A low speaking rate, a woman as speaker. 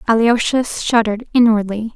Yes: slow, 90 wpm; female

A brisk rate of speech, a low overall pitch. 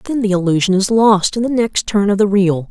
No: fast, 265 wpm; high, 200 Hz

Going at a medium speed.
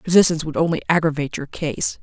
Yes: average, 180 wpm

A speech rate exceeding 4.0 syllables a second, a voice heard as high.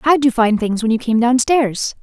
Yes: 4.6 syllables/s; high, 240 Hz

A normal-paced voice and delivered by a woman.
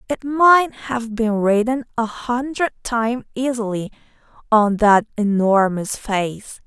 No: slow, 115 wpm; female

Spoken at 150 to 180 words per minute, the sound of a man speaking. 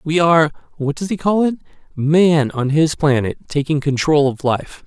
Yes: average, 160 wpm; male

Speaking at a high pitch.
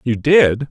No: low, 135 Hz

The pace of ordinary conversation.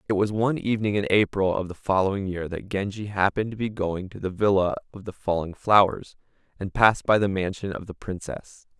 No: fast, 210 wpm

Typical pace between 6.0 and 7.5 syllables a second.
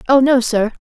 No: 5.4 syllables/s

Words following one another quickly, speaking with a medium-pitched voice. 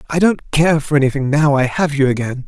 Yes: fast, 240 wpm; medium, 145 Hz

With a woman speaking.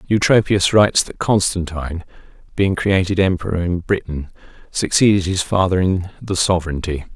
No: male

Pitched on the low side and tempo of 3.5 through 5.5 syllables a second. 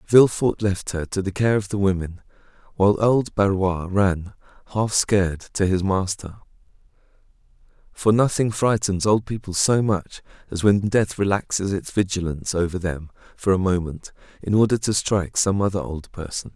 Yes: low, 100 Hz; 5.0 syllables/s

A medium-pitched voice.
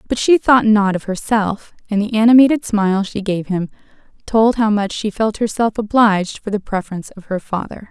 No: high, 210 Hz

